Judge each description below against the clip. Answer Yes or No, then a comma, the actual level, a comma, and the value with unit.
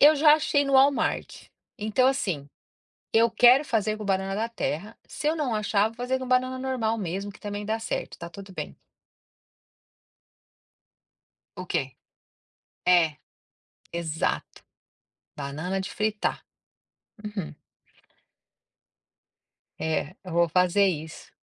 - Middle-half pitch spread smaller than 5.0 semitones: No, wide, 5.6 semitones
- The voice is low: No, high, 210 Hz